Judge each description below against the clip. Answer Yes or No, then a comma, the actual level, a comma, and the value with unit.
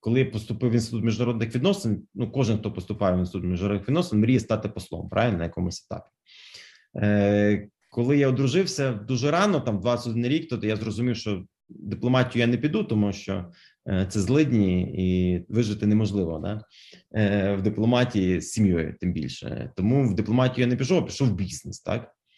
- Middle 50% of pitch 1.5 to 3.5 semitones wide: No, average, 3.9 semitones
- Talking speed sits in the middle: No, fast, 175 wpm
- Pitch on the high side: No, low, 110 Hz